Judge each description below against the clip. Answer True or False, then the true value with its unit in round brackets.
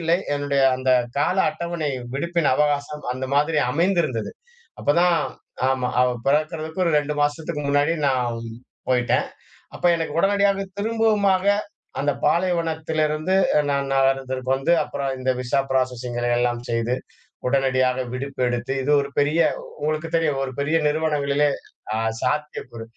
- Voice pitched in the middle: True (145 Hz)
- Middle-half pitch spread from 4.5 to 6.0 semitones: False (3.9 semitones)